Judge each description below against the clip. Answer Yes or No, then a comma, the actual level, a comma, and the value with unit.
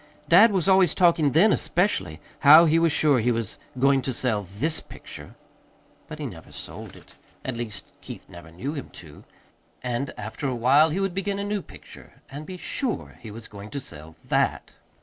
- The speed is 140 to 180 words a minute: No, average, 190 wpm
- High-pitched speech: No, medium, 140 Hz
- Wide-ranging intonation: Yes, wide, 7.1 semitones